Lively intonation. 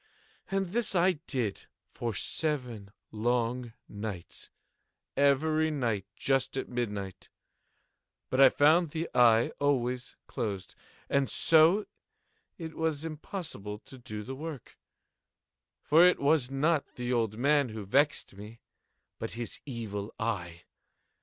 Yes: wide, 5.7 semitones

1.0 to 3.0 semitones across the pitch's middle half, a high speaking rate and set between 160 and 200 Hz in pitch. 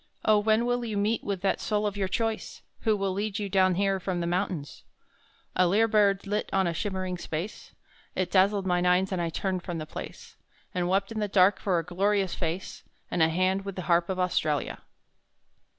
Yes: narrow, 2.4 semitones; fast, 210 wpm; high, 190 Hz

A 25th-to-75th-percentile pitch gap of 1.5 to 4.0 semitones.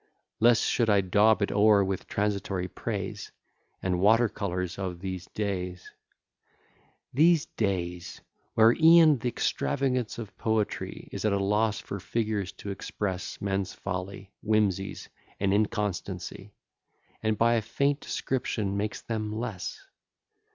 Yes: narrow, 2.6 semitones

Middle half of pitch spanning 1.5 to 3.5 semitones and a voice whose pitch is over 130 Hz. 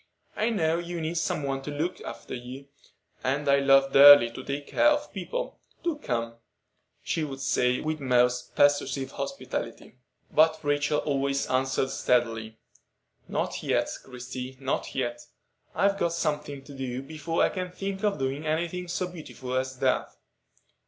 No: average, 4.1 semitones; medium, 140 Hz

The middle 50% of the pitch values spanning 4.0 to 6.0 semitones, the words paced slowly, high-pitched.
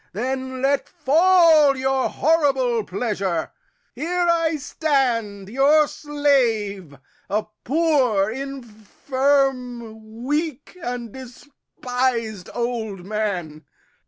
Yes: average, 4.8 semitones; slow, 80 wpm; very high, 255 Hz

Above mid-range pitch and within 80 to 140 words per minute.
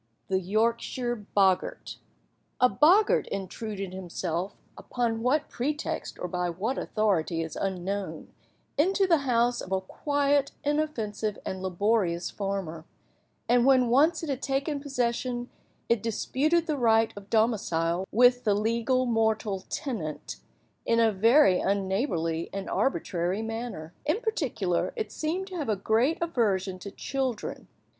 Yes: high, 225 Hz; slow, 135 wpm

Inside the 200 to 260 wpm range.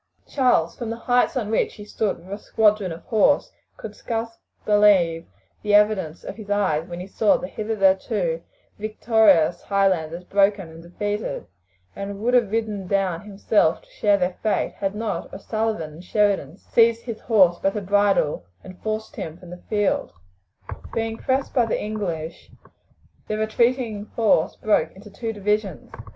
No: average, 160 wpm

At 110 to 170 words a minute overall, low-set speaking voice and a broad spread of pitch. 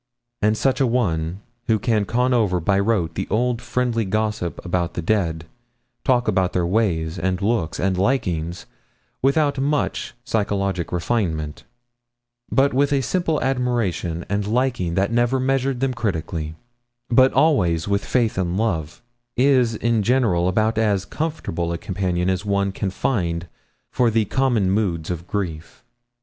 Yes: average, 150 wpm; low, 105 Hz; wide, 5.7 semitones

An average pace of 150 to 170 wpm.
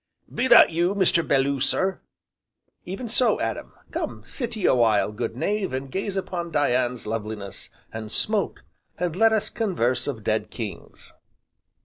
Yes: average, 155 wpm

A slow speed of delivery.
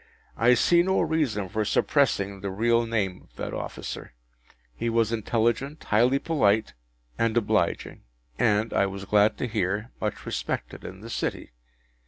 No: average, 150 wpm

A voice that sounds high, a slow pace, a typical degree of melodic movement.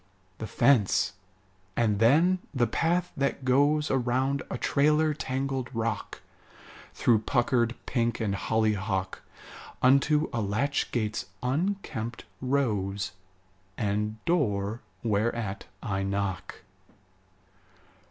No: low, 120 Hz; slow, 95 wpm; average, 4.8 semitones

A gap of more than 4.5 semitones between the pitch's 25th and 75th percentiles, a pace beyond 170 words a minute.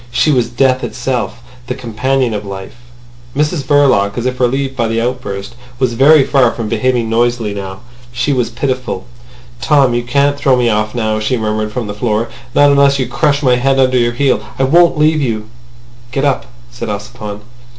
No: average, 3.2 semitones; average, 180 wpm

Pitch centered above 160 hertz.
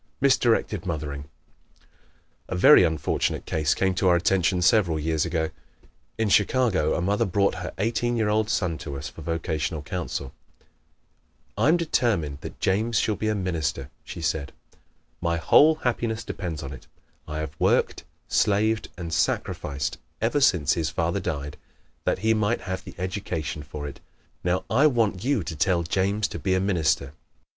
No: very low, 90 Hz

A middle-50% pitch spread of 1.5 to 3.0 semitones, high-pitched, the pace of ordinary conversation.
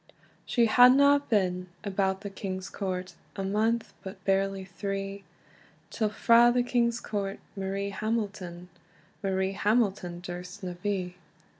No: narrow, 2.5 semitones; high, 195 Hz; slow, 125 wpm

